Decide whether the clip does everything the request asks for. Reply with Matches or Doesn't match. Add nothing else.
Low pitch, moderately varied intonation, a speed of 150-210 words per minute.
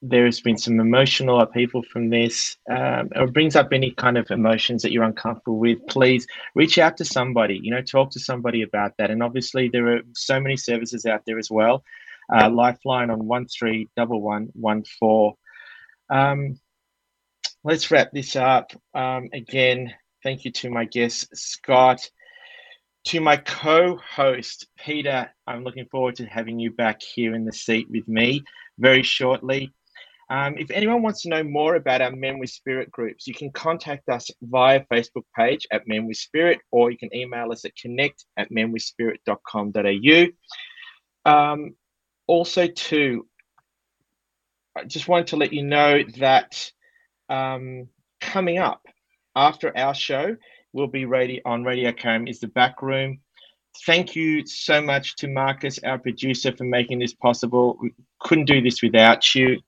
Matches